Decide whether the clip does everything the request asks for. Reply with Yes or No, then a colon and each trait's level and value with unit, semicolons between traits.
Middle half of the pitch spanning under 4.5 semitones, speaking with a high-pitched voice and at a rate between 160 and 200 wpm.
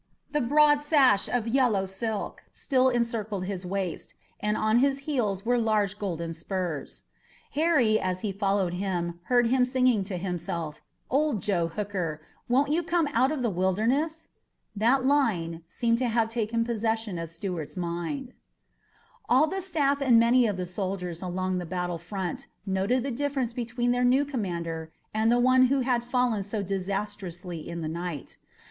No: wide, 5.6 semitones; high, 215 Hz; average, 165 wpm